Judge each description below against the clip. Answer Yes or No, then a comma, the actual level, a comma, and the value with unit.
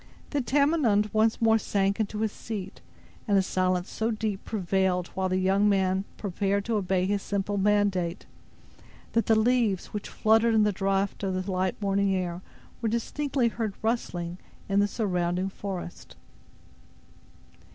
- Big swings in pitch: No, narrow, 2.6 semitones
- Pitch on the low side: No, high, 200 Hz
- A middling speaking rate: Yes, average, 150 wpm